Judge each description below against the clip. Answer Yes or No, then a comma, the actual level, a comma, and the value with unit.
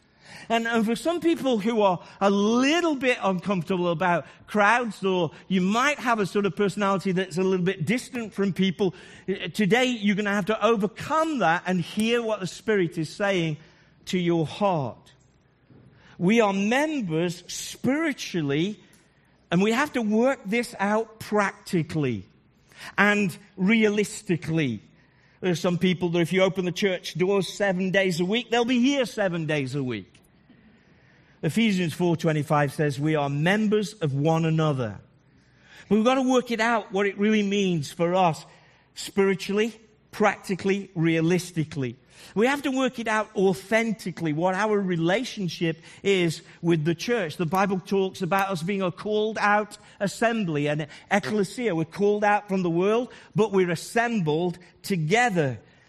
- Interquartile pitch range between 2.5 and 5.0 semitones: Yes, average, 4.0 semitones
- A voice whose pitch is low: No, high, 195 Hz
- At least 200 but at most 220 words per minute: No, average, 155 wpm